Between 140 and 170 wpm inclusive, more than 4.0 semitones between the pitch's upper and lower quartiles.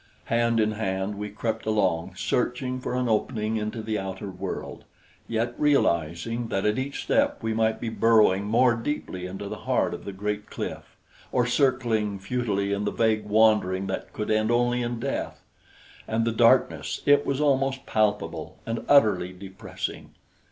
No: average, 165 wpm; average, 3.0 semitones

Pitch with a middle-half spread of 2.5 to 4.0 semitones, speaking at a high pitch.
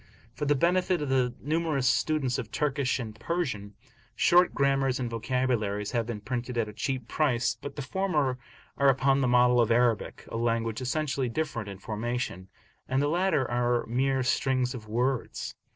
No: average, 3.1 semitones; low, 130 Hz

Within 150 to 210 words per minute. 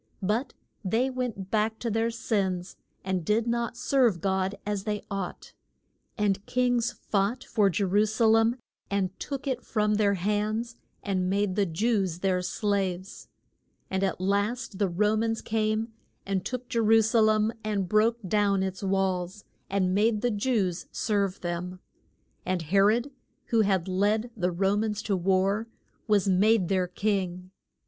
Yes: average, 160 wpm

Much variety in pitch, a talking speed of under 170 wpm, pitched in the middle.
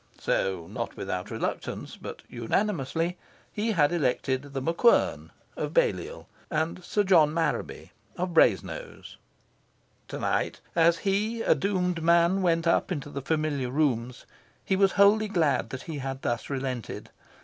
Yes: wide, 6.0 semitones; average, 140 wpm; medium, 165 Hz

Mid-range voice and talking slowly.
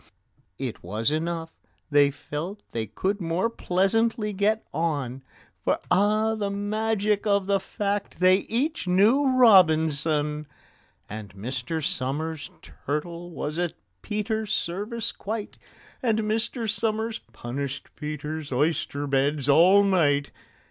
Yes: medium, 175 Hz; slow, 115 wpm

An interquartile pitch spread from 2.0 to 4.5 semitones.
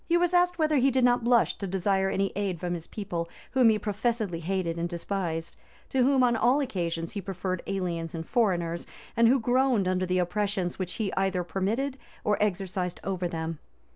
No: average, 5.2 semitones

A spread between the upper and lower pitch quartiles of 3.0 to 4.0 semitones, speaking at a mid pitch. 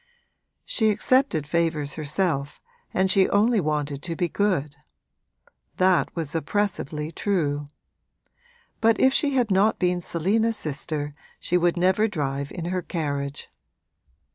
No: average, 5.3 semitones; medium, 175 Hz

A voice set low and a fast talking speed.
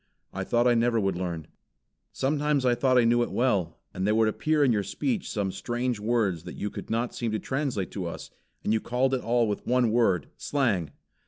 Yes: low, 120 Hz; fast, 220 wpm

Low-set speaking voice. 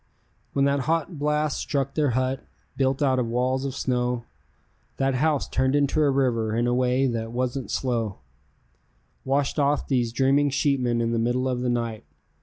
Yes: low, 130 Hz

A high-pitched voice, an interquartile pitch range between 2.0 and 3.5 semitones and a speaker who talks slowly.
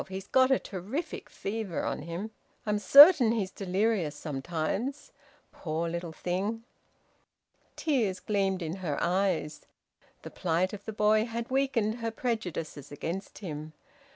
No: high, 195 Hz; average, 5.0 semitones; slow, 130 wpm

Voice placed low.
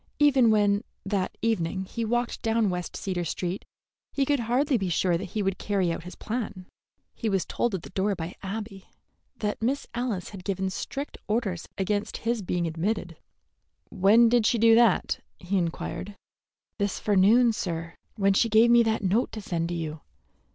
No: high, 205 Hz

